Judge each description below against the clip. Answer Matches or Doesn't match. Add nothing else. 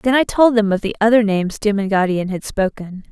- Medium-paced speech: Doesn't match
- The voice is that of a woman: Matches